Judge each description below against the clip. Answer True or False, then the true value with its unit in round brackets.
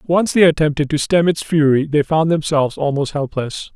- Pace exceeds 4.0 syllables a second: True (5.3 syllables/s)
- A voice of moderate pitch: True (150 Hz)